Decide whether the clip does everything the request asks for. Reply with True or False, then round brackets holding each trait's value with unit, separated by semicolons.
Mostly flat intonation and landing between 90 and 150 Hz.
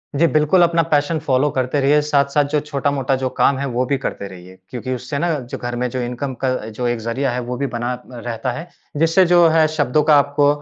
False (3.2 semitones; 140 Hz)